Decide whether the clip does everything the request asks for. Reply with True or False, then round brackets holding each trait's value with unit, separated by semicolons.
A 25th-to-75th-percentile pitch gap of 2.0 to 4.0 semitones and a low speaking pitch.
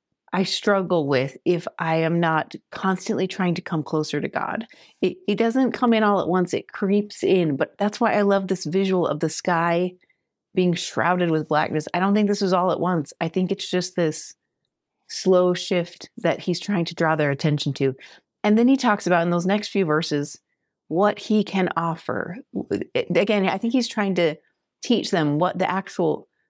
False (3.5 semitones; 180 Hz)